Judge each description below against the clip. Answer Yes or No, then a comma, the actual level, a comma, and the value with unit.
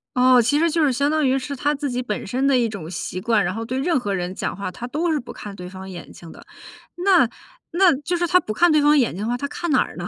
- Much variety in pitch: Yes, wide, 6.6 semitones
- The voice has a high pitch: Yes, very high, 255 Hz